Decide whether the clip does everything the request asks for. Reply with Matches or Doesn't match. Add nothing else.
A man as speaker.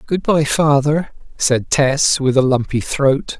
Matches